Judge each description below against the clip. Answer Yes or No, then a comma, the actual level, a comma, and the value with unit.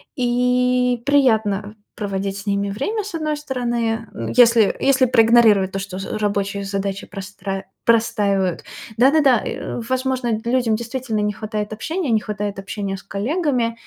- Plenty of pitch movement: No, average, 3.9 semitones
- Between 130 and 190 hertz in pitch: No, high, 225 Hz